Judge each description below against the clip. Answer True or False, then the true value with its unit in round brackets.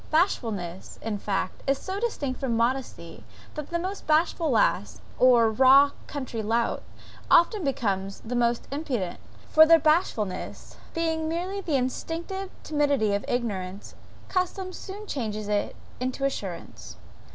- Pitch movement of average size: False (7.3 semitones)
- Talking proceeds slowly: True (130 wpm)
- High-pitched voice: True (260 Hz)